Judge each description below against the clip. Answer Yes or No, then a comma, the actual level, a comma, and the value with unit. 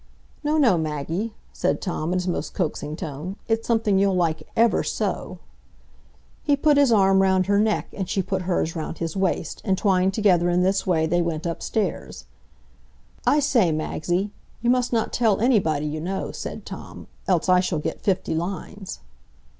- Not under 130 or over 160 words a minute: No, average, 175 wpm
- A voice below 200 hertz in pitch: Yes, high, 190 Hz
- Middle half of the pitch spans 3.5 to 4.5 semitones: Yes, average, 4.1 semitones